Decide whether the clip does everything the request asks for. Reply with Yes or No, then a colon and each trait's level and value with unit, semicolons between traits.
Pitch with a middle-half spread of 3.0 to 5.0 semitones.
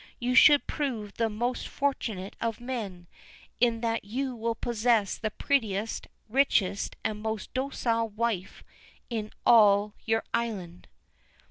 No: narrow, 2.5 semitones